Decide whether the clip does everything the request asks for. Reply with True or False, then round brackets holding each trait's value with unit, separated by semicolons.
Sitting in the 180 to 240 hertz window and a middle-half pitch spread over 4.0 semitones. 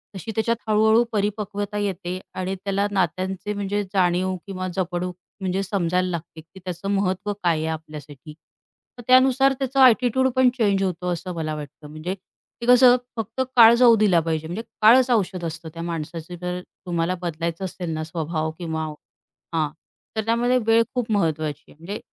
True (185 Hz; 4.5 semitones)